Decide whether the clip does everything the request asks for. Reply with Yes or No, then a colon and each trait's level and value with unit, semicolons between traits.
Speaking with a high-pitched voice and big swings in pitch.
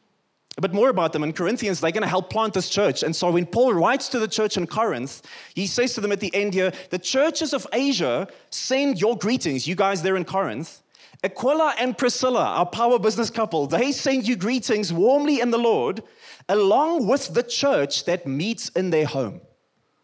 Yes: high, 215 Hz; wide, 5.7 semitones